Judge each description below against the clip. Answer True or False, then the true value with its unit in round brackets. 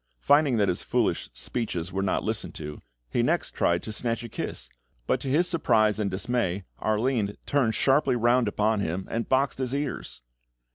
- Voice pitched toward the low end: True (110 Hz)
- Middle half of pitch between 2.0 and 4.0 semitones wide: False (4.7 semitones)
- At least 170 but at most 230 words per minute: True (180 wpm)